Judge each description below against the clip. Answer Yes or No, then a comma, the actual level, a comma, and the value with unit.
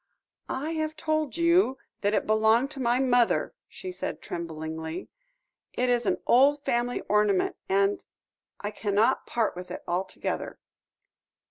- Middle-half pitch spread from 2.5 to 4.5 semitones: No, wide, 5.6 semitones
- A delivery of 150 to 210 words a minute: No, slow, 135 wpm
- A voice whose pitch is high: Yes, high, 235 Hz